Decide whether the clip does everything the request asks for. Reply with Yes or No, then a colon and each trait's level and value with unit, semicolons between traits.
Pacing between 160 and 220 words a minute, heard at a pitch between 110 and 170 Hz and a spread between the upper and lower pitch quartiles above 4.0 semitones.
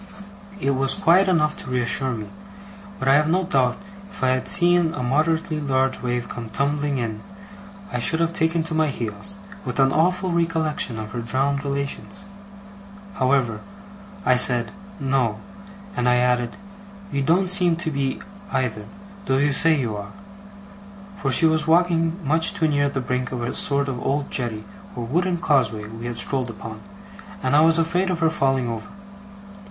Yes: average, 175 wpm; medium, 140 Hz; average, 4.7 semitones